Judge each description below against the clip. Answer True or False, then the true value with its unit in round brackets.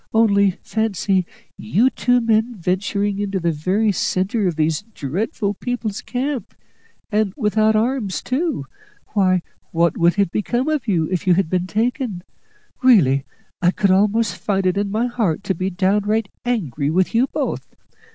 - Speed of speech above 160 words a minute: False (155 wpm)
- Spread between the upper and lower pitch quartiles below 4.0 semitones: True (3.5 semitones)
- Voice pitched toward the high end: True (200 Hz)